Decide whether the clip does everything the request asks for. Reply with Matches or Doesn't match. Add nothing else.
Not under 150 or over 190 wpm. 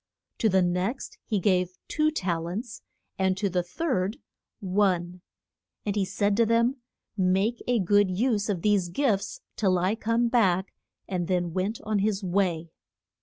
Matches